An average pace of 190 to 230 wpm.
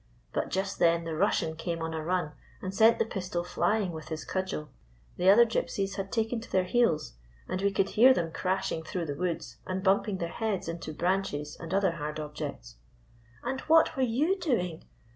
Yes: average, 200 wpm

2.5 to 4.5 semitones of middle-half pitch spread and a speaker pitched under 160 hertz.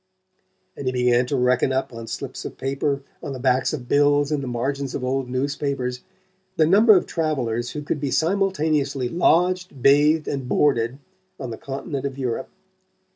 Yes: average, 2.8 semitones; medium, 140 Hz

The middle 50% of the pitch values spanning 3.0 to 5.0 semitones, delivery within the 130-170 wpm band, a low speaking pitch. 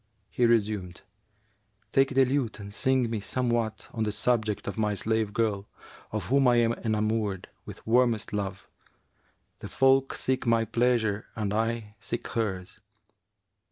No: narrow, 2.6 semitones; average, 145 wpm; low, 110 Hz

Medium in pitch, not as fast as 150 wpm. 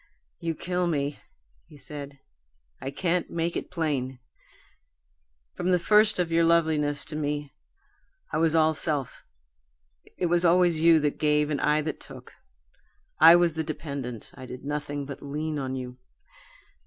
No: medium, 155 Hz; average, 155 wpm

